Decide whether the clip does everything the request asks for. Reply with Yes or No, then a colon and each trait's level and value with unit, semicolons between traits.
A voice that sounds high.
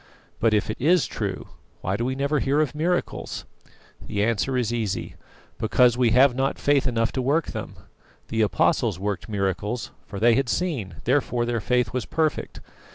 No: low, 120 Hz